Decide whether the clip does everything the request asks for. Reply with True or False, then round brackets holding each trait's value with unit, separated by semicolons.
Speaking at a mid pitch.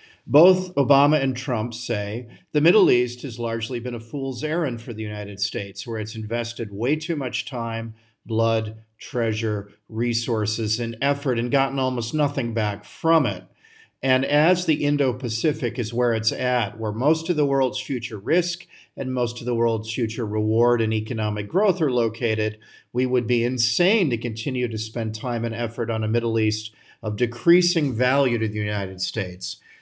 False (120 Hz)